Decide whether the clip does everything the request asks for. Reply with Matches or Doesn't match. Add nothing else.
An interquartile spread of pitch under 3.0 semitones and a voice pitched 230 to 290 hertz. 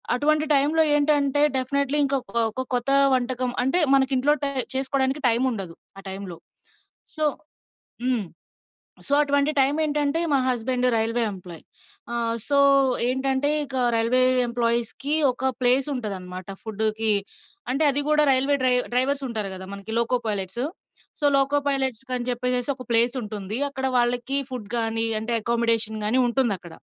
Doesn't match